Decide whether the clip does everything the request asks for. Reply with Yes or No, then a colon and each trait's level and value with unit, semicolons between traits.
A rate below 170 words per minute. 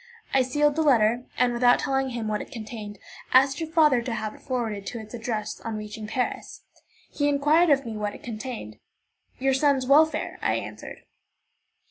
No: average, 180 wpm